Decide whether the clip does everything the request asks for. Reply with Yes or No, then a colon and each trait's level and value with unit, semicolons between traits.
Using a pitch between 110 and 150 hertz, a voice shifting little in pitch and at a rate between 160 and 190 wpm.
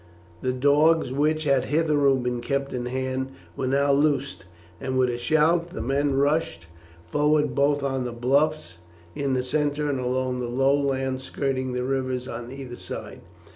Yes: low, 135 Hz; narrow, 2.1 semitones; average, 170 wpm